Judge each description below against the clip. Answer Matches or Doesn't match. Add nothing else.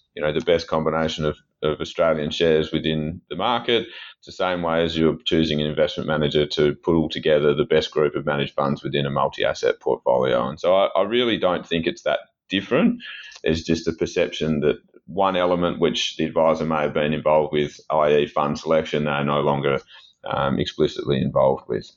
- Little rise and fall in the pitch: Matches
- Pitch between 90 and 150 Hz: Doesn't match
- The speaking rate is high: Doesn't match